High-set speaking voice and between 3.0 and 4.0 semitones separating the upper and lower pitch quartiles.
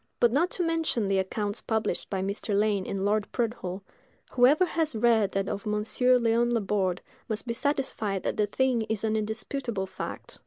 Yes: high, 220 Hz; average, 3.4 semitones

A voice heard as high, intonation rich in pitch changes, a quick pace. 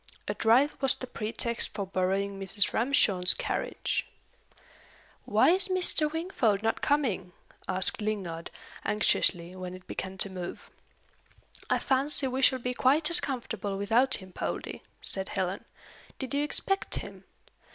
No: high, 220 Hz; wide, 6.1 semitones; average, 140 wpm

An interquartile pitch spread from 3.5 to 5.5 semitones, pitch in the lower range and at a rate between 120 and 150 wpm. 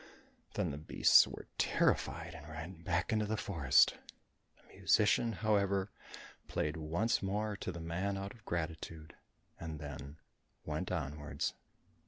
Yes: average, 4.4 semitones; very low, 85 Hz; slow, 135 wpm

